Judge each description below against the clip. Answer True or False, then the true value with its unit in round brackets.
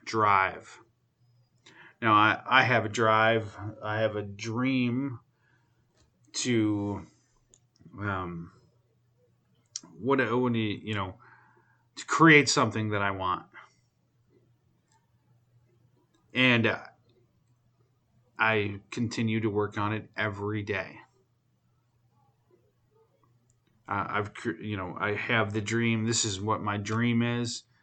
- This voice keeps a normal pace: False (100 wpm)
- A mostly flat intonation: True (2.2 semitones)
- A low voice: True (115 Hz)